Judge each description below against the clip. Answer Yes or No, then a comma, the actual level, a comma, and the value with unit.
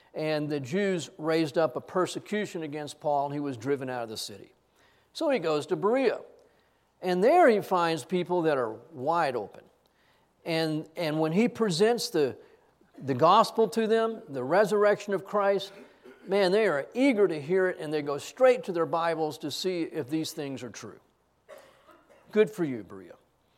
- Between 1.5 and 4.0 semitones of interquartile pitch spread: No, wide, 5.4 semitones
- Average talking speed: Yes, average, 180 wpm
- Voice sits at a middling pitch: Yes, medium, 170 Hz